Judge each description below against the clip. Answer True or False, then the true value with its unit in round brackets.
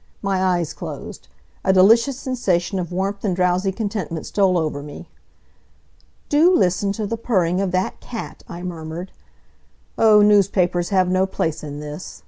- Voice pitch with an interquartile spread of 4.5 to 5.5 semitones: False (2.8 semitones)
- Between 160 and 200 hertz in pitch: True (185 Hz)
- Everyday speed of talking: True (150 wpm)